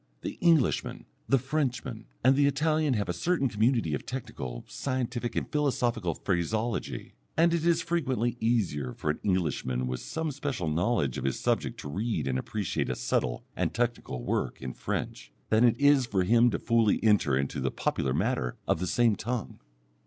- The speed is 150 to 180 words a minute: Yes, average, 175 wpm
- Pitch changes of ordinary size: No, wide, 8.3 semitones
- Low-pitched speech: Yes, low, 115 Hz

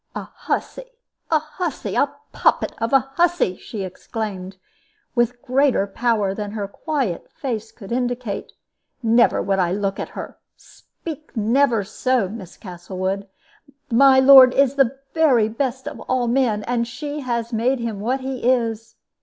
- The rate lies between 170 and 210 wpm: No, average, 150 wpm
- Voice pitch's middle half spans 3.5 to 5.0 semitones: Yes, average, 4.3 semitones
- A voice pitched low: No, high, 235 Hz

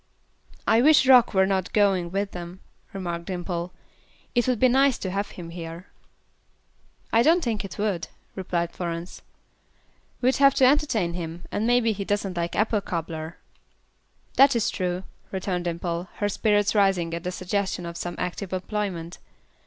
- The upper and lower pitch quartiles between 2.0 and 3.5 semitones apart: No, average, 3.9 semitones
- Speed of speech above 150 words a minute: Yes, average, 160 wpm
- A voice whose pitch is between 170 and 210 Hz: Yes, high, 190 Hz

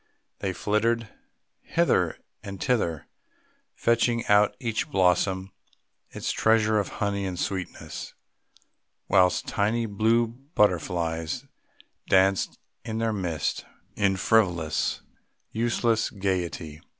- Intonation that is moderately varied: Yes, average, 3.6 semitones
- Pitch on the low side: Yes, low, 100 Hz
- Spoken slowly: Yes, slow, 100 wpm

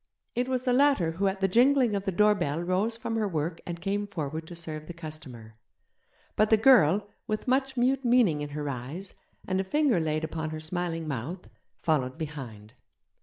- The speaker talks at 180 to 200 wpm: Yes, average, 190 wpm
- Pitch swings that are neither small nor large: No, wide, 6.0 semitones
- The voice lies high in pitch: No, medium, 175 Hz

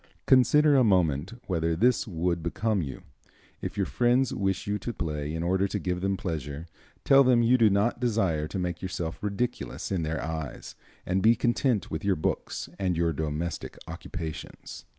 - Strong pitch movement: Yes, wide, 5.8 semitones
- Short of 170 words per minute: No, average, 175 wpm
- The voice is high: No, very low, 95 Hz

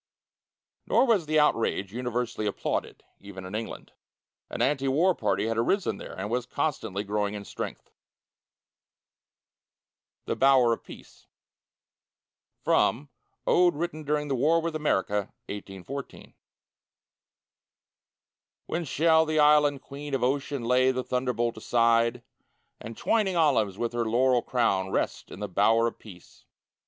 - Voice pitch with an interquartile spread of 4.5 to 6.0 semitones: Yes, average, 5.1 semitones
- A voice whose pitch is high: No, low, 125 Hz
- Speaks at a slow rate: Yes, slow, 130 wpm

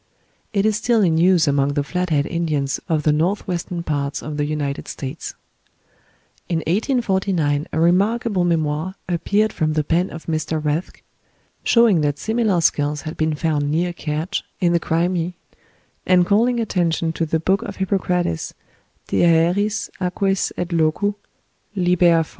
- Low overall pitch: No, medium, 170 Hz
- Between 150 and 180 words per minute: Yes, average, 155 wpm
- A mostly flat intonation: No, average, 3.5 semitones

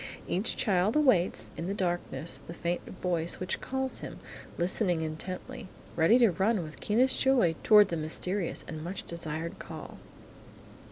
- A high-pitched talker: No, medium, 180 Hz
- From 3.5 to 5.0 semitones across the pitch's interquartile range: Yes, average, 4.2 semitones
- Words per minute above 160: No, average, 150 wpm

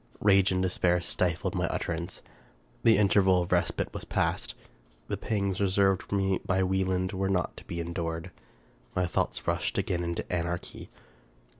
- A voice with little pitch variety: Yes, narrow, 1.9 semitones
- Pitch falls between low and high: No, very low, 95 Hz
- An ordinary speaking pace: Yes, average, 155 wpm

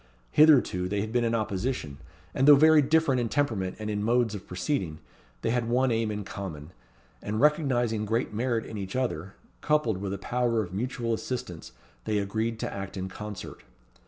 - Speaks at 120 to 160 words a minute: No, average, 185 wpm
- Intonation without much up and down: No, average, 4.0 semitones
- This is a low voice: Yes, low, 110 Hz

